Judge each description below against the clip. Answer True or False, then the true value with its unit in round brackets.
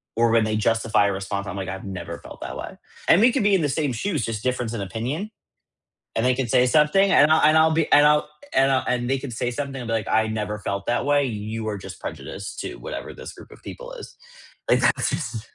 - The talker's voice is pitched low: True (125 Hz)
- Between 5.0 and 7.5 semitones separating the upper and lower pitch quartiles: True (5.6 semitones)